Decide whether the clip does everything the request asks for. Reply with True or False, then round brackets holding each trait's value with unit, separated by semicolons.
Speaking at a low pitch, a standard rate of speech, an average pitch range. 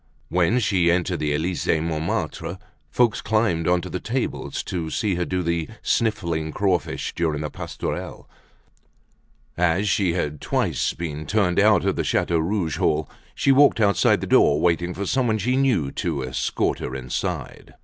True (85 Hz; 160 wpm; 4.2 semitones)